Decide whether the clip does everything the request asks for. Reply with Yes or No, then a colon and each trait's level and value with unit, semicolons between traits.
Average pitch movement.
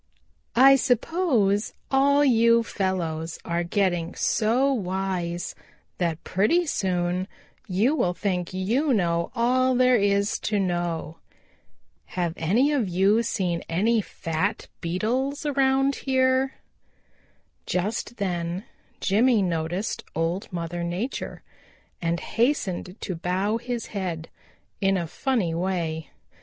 No: wide, 5.9 semitones